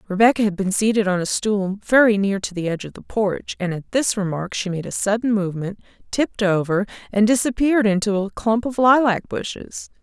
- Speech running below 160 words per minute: No, fast, 205 wpm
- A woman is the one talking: Yes, female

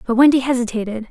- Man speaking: No, female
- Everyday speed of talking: Yes, average, 160 wpm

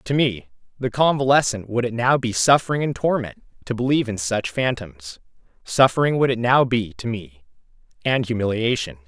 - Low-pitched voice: Yes, low, 115 Hz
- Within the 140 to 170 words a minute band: Yes, average, 165 wpm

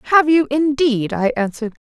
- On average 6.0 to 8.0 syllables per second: No, 5.5 syllables/s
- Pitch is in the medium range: No, very high, 275 Hz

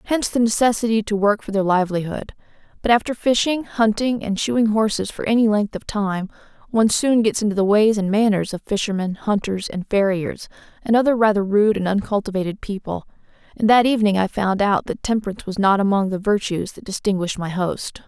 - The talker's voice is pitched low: No, high, 210 Hz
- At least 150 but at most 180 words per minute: No, average, 190 wpm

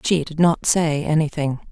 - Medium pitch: Yes, medium, 155 Hz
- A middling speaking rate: Yes, average, 175 wpm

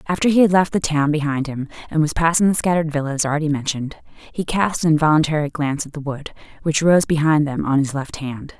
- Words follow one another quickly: Yes, fast, 225 wpm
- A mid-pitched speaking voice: Yes, medium, 155 Hz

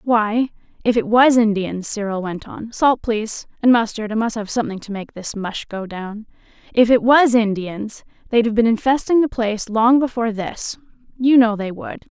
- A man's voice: No, female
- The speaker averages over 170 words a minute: Yes, average, 190 wpm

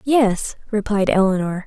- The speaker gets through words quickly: No, slow, 110 wpm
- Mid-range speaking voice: No, high, 205 Hz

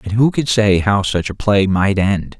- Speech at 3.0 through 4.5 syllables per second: Yes, 4.4 syllables/s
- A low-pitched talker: Yes, low, 105 Hz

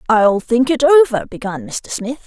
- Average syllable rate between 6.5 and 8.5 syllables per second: No, 5.1 syllables/s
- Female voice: Yes, female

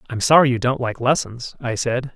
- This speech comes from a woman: No, male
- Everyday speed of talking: No, fast, 225 wpm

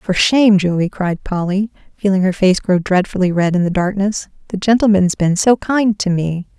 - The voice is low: No, high, 190 Hz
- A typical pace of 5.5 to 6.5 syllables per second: No, 4.8 syllables/s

